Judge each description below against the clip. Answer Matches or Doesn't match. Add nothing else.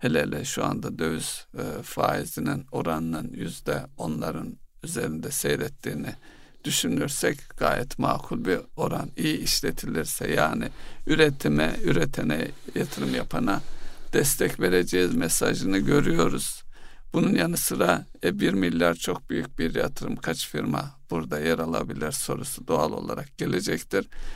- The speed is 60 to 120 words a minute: Matches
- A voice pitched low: Matches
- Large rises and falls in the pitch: Doesn't match